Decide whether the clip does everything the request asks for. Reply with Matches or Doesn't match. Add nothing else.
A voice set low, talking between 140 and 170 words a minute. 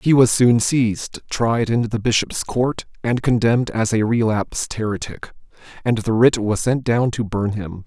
Doesn't match